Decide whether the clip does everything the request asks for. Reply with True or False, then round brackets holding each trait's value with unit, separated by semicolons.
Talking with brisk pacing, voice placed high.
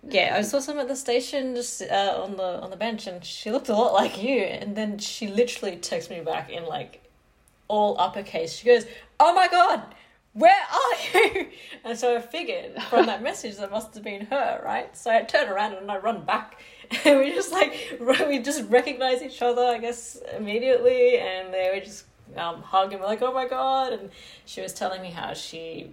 True (215 wpm; 235 Hz)